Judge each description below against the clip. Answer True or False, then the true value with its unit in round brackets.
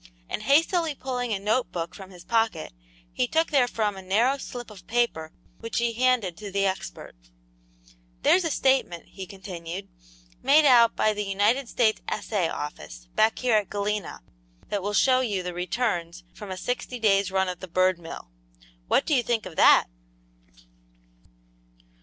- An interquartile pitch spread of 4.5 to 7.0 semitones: True (4.8 semitones)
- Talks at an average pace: True (165 wpm)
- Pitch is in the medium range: False (210 Hz)